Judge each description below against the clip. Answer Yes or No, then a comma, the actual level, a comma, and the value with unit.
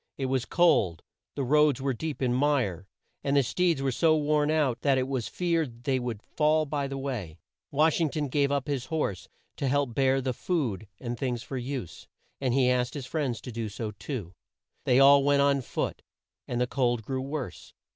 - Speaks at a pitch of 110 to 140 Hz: Yes, low, 135 Hz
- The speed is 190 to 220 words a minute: Yes, fast, 205 wpm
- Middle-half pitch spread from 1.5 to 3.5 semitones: Yes, average, 3.0 semitones